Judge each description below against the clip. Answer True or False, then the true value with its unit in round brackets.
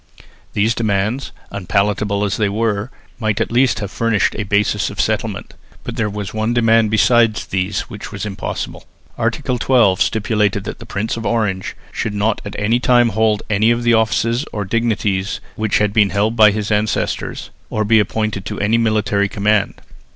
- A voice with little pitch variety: True (1.9 semitones)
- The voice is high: False (110 Hz)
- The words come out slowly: False (175 wpm)